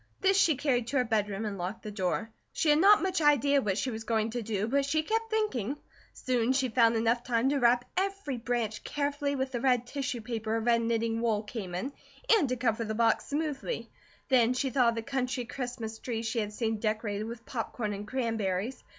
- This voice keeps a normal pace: No, fast, 215 wpm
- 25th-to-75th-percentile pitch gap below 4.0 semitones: Yes, average, 3.6 semitones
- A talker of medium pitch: No, high, 240 Hz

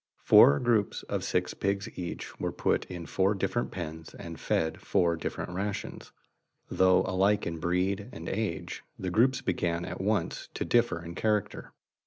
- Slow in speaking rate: No, average, 160 wpm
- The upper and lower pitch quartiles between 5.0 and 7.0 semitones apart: No, average, 3.4 semitones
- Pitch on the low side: Yes, very low, 95 Hz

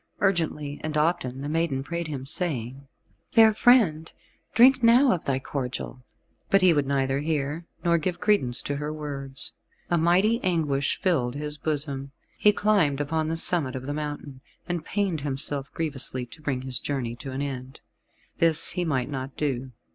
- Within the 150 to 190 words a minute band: Yes, average, 170 wpm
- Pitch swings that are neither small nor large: Yes, average, 4.0 semitones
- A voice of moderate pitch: Yes, medium, 150 Hz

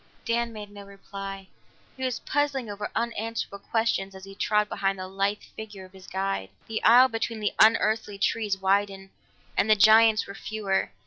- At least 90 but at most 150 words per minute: No, average, 175 wpm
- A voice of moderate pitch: No, high, 205 Hz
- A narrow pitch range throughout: Yes, narrow, 2.3 semitones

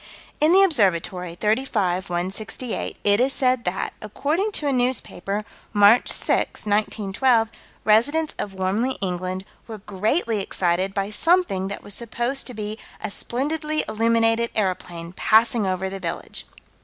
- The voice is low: No, high, 215 Hz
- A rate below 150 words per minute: Yes, slow, 135 wpm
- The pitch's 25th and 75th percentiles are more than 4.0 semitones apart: Yes, average, 4.6 semitones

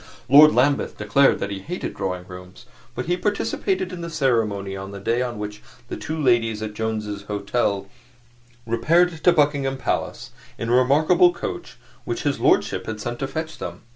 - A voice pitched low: Yes, low, 120 Hz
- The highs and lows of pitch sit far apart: Yes, wide, 6.8 semitones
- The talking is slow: No, average, 175 wpm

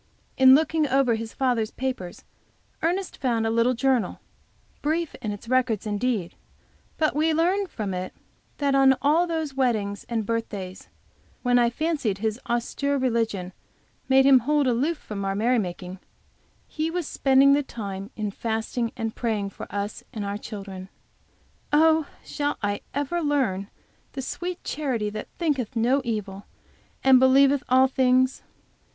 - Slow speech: No, average, 150 wpm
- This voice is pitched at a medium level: No, very high, 250 Hz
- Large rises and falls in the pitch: No, average, 4.9 semitones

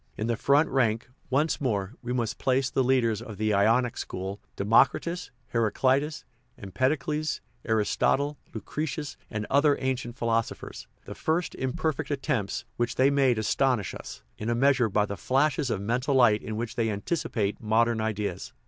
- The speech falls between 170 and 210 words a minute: No, average, 160 wpm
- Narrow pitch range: No, average, 4.0 semitones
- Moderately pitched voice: No, low, 120 Hz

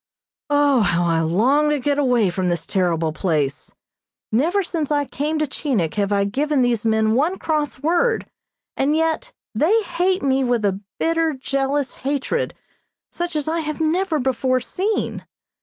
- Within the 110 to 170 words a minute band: Yes, average, 160 wpm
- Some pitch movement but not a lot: No, wide, 6.5 semitones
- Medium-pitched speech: No, very high, 275 Hz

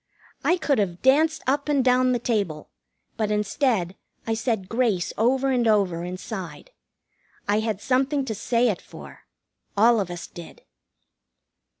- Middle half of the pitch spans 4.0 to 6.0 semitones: Yes, average, 4.9 semitones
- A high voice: Yes, high, 225 Hz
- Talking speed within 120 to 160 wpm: Yes, average, 145 wpm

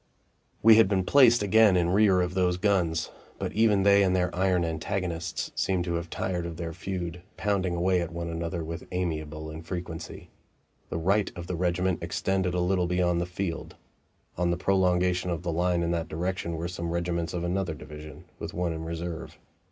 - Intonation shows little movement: Yes, narrow, 1.8 semitones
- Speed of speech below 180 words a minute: No, average, 190 wpm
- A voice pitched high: No, very low, 90 Hz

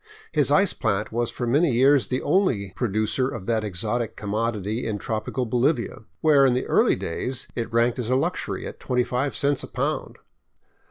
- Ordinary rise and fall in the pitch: Yes, average, 3.2 semitones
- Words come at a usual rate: Yes, average, 175 wpm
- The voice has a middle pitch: No, low, 120 Hz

